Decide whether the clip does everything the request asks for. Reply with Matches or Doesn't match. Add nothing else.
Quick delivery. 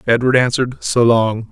Doesn't match